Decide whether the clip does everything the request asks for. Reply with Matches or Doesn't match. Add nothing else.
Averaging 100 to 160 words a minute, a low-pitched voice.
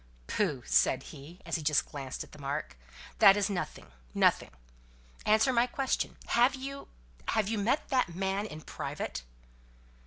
Doesn't match